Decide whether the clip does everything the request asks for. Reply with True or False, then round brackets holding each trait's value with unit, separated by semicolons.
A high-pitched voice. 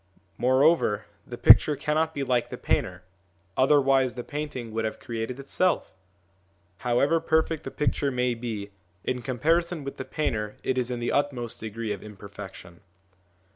False (125 Hz)